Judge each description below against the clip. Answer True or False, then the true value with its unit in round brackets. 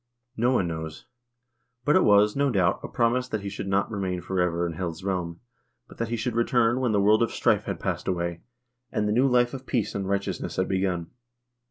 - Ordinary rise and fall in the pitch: True (4.6 semitones)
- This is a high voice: False (100 Hz)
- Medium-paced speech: False (220 wpm)